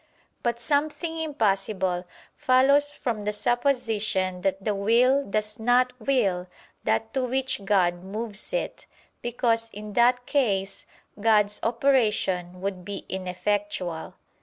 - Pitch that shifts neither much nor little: Yes, average, 4.4 semitones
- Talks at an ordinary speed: No, slow, 115 wpm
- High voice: Yes, high, 215 Hz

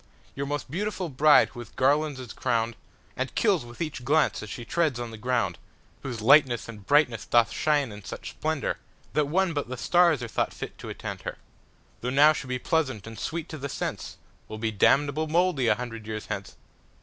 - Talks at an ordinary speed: Yes, average, 185 wpm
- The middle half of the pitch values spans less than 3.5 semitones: No, average, 4.6 semitones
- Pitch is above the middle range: No, low, 130 Hz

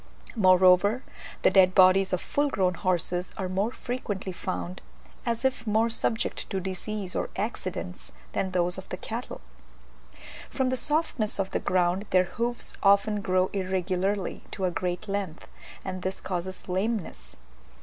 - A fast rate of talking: No, average, 150 wpm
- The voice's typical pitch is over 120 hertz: Yes, high, 190 Hz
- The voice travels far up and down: No, average, 2.7 semitones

